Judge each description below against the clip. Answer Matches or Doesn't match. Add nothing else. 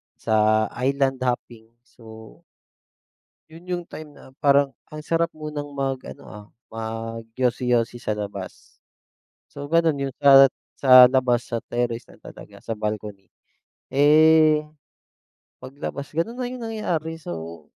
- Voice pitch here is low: Matches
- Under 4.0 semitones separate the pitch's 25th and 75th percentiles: Doesn't match